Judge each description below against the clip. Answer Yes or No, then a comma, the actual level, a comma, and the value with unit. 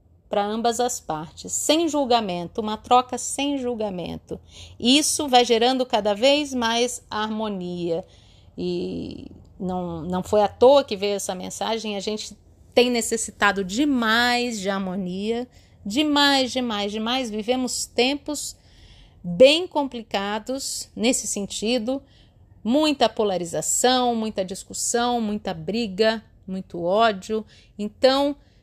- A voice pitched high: Yes, high, 220 Hz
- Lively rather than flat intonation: No, average, 4.1 semitones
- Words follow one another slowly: Yes, slow, 110 wpm